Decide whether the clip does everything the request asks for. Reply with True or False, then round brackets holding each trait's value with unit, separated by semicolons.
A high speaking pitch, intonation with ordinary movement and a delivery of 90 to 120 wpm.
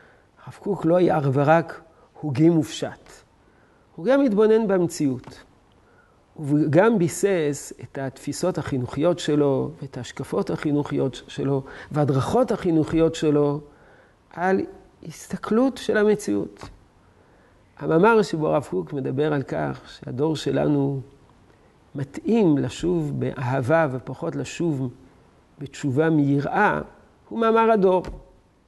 False (150 Hz; 4.4 semitones; 105 wpm)